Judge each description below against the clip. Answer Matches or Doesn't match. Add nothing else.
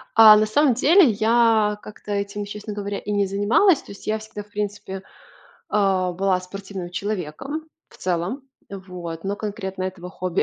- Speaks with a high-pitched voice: Matches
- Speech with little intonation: Matches